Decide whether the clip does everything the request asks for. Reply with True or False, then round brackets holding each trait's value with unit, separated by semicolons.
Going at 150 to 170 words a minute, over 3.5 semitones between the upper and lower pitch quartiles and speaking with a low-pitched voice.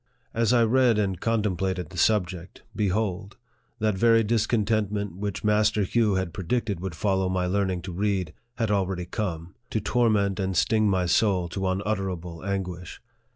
False (155 wpm; 2.8 semitones; 100 Hz)